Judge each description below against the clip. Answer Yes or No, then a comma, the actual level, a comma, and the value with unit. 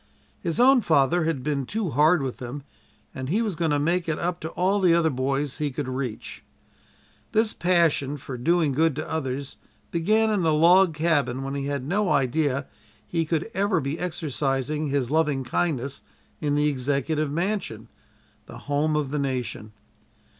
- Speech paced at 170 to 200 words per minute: Yes, average, 175 wpm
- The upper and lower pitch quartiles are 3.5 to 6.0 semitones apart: Yes, average, 3.9 semitones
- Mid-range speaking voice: Yes, medium, 150 Hz